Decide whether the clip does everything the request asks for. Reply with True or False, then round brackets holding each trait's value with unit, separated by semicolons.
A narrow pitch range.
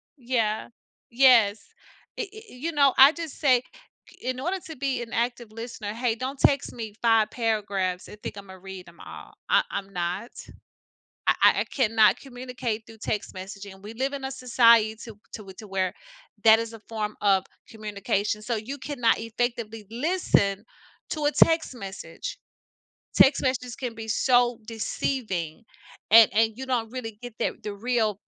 False (3.3 semitones)